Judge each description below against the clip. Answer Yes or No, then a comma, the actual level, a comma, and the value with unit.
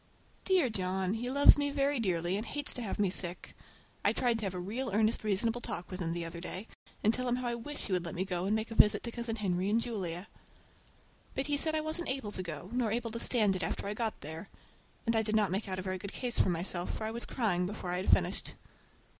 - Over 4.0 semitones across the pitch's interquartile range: Yes, average, 4.6 semitones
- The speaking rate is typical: No, fast, 265 wpm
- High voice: Yes, high, 215 Hz